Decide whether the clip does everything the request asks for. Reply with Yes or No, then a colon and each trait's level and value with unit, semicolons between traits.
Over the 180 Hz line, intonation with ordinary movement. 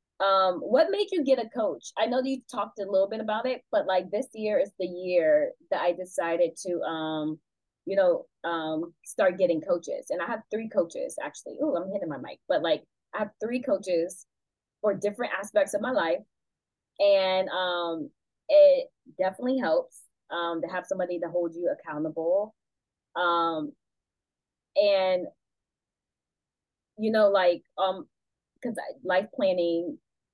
No: high, 190 Hz; wide, 5.7 semitones